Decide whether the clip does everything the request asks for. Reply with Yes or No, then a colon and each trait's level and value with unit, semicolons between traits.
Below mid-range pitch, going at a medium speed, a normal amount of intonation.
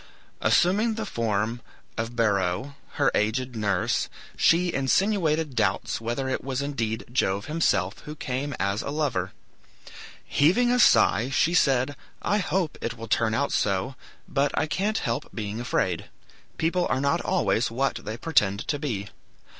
No: low, 130 Hz; average, 150 wpm; wide, 6.0 semitones